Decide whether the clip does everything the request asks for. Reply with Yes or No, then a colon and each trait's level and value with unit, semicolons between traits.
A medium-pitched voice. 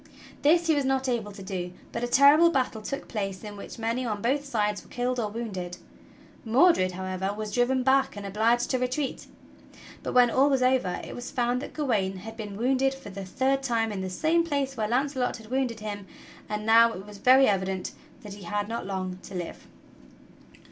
No: high, 230 Hz